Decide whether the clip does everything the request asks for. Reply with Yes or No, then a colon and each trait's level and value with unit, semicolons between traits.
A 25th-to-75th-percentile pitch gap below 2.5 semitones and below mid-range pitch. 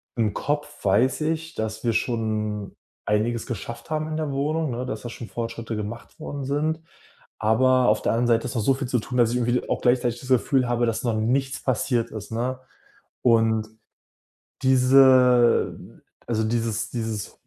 No: average, 2.8 semitones; low, 120 Hz